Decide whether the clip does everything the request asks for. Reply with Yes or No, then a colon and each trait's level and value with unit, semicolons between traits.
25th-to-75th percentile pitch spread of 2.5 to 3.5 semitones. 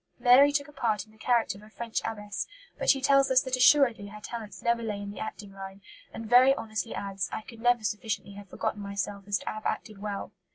Yes: average, 3.2 semitones